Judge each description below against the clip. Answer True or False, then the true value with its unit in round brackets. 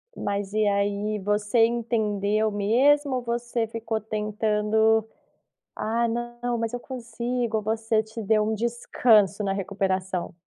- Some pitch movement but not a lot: False (2.3 semitones)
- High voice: True (220 Hz)